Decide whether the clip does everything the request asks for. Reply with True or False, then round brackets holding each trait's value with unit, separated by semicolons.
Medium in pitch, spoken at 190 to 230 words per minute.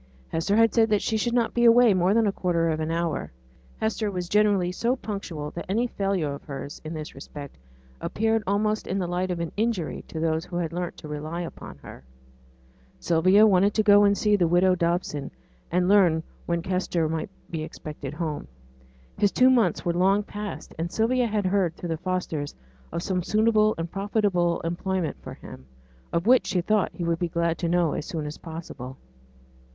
True (180 Hz; 200 wpm)